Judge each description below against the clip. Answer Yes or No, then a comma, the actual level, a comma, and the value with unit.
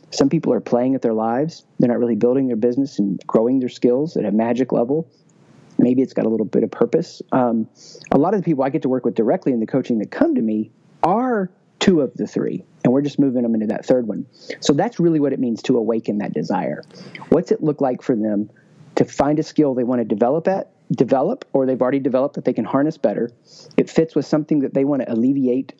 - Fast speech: Yes, fast, 245 wpm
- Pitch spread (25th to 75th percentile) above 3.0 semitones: Yes, average, 4.2 semitones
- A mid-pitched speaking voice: No, low, 130 Hz